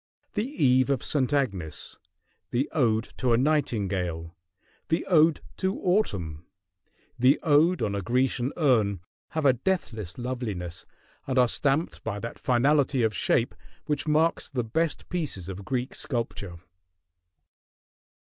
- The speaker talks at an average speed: No, slow, 130 wpm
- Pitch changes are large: Yes, wide, 6.3 semitones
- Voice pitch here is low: Yes, low, 125 Hz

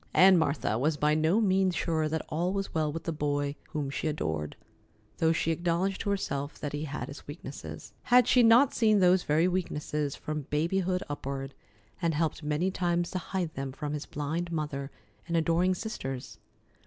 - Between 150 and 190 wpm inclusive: Yes, average, 180 wpm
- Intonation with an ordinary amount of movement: Yes, average, 3.7 semitones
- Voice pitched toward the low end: No, medium, 160 Hz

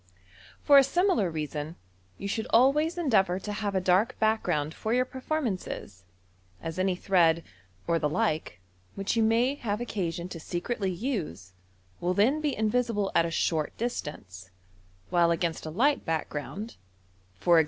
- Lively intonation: Yes, wide, 6.3 semitones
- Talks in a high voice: Yes, high, 195 Hz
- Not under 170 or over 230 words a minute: No, average, 155 wpm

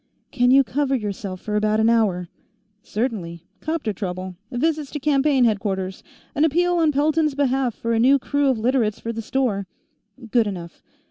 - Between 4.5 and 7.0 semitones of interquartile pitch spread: Yes, average, 5.2 semitones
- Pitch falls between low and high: No, high, 240 Hz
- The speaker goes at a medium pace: Yes, average, 175 wpm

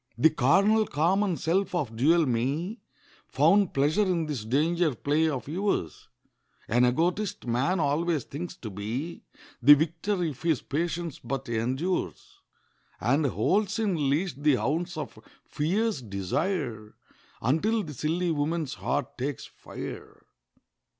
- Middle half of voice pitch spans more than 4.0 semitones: Yes, average, 4.9 semitones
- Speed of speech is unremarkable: No, slow, 130 wpm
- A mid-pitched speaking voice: Yes, medium, 155 Hz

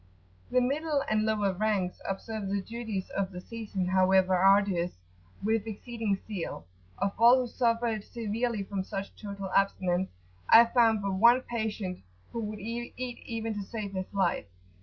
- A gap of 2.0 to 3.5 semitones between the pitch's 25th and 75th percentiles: Yes, average, 3.1 semitones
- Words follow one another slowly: No, average, 155 wpm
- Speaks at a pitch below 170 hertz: No, high, 210 Hz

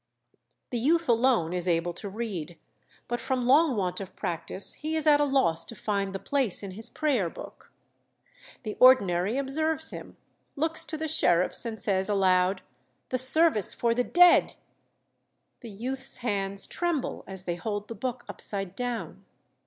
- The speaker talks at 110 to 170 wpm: Yes, average, 160 wpm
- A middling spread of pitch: No, wide, 5.9 semitones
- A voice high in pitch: Yes, high, 230 Hz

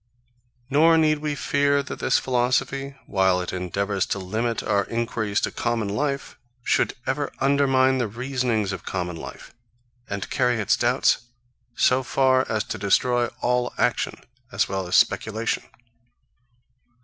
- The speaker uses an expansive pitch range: No, average, 4.9 semitones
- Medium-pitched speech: No, low, 120 Hz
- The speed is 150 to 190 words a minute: No, average, 140 wpm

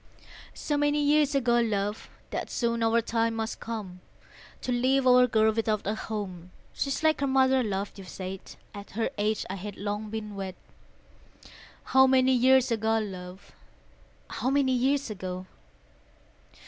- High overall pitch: Yes, high, 225 Hz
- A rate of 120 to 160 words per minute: Yes, average, 150 wpm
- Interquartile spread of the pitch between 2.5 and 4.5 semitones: Yes, average, 4.2 semitones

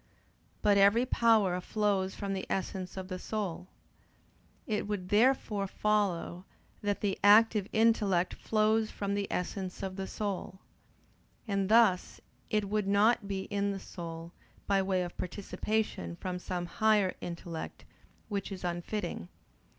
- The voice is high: Yes, high, 200 Hz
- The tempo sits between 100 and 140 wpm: Yes, slow, 135 wpm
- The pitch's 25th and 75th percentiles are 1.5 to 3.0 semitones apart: Yes, narrow, 2.5 semitones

